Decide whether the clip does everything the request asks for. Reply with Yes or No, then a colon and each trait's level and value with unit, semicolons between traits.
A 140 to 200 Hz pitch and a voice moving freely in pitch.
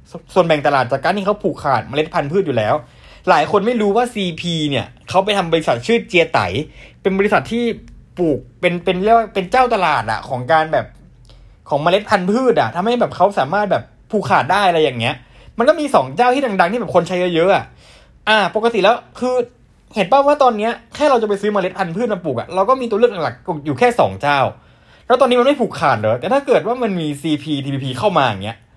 Yes: high, 190 Hz; wide, 7.4 semitones